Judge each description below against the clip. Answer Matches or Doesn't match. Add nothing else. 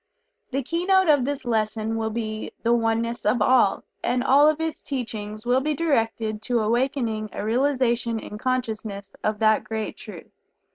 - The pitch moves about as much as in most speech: Matches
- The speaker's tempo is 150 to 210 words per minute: Matches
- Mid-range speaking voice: Doesn't match